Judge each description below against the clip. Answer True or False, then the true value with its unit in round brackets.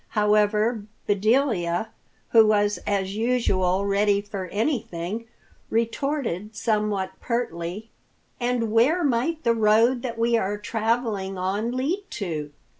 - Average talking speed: False (115 wpm)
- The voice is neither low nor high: False (215 Hz)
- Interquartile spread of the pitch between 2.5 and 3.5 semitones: True (2.9 semitones)